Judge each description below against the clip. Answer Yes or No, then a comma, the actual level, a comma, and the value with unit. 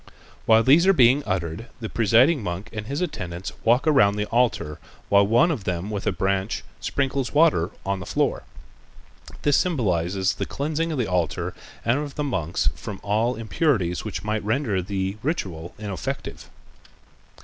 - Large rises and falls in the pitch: Yes, wide, 6.3 semitones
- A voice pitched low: Yes, low, 110 Hz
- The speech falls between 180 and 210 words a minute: No, average, 160 wpm